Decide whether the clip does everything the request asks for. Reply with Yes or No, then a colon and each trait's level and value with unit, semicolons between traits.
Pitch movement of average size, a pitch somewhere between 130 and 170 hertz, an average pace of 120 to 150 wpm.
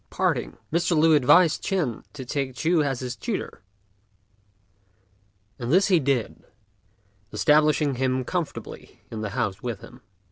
Yes: average, 4.5 semitones; medium, 140 Hz; average, 140 wpm